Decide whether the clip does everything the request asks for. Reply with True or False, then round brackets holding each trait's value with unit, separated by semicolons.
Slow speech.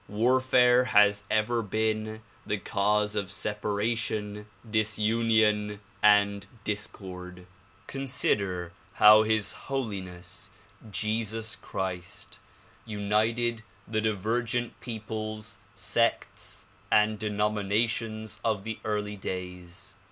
True (85 wpm)